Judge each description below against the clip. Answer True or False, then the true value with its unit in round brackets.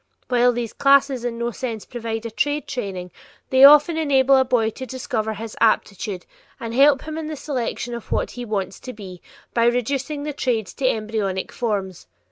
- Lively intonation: False (3.7 semitones)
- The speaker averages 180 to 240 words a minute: True (185 wpm)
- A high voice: True (240 Hz)